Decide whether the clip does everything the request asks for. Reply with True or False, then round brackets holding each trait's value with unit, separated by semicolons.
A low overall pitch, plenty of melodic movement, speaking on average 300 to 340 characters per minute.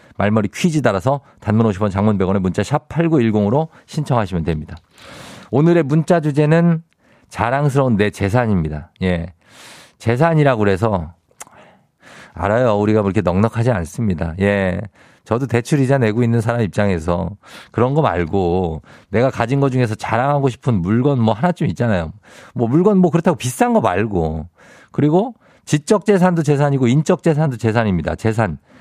True (115 Hz; 6.5 semitones; 325 characters per minute)